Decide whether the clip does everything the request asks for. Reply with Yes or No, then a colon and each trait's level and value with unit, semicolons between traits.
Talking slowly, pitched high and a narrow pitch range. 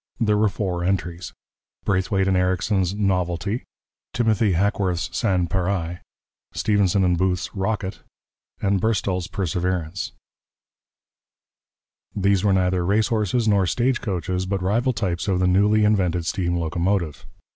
No: slow, 115 wpm; very low, 95 Hz; narrow, 2.2 semitones